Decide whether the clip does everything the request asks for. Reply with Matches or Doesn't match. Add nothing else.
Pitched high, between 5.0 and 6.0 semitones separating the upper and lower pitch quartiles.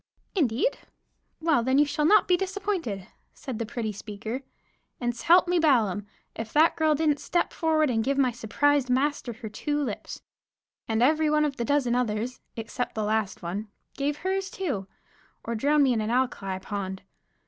Matches